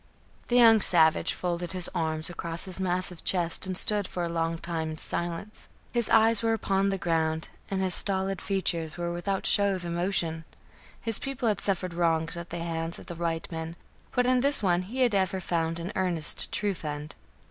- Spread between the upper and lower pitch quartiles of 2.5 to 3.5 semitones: Yes, average, 3.0 semitones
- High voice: No, medium, 175 Hz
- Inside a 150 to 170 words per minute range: No, average, 195 wpm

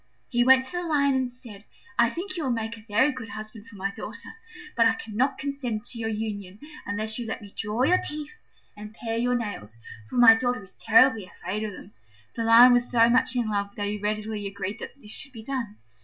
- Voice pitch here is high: Yes, high, 225 Hz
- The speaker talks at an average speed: No, fast, 230 wpm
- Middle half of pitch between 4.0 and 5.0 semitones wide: No, average, 3.1 semitones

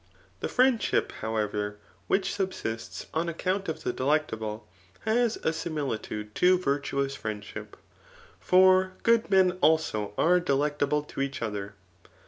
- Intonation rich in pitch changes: Yes, wide, 8.8 semitones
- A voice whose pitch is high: No, medium, 150 Hz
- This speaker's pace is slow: Yes, slow, 120 wpm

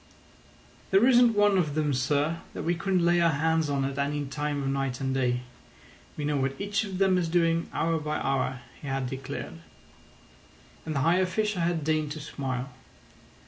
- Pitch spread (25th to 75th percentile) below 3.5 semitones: No, average, 4.2 semitones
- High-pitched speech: No, medium, 150 Hz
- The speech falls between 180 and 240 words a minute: Yes, average, 185 wpm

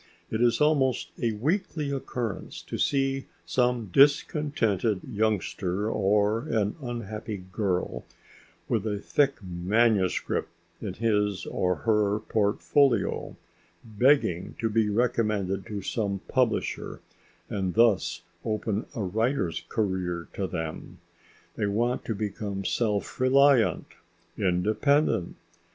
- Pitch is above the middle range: No, low, 110 Hz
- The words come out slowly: Yes, slow, 105 wpm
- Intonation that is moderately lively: Yes, average, 3.6 semitones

